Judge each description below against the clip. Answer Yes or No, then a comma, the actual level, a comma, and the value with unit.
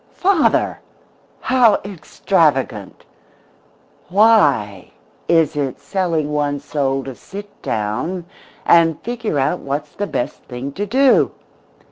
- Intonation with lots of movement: Yes, wide, 6.9 semitones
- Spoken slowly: Yes, slow, 105 wpm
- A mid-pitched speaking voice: Yes, medium, 155 Hz